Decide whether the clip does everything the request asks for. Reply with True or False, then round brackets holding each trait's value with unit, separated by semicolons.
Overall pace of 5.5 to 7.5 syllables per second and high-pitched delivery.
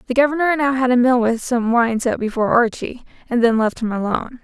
True (6.0 syllables/s; 240 Hz)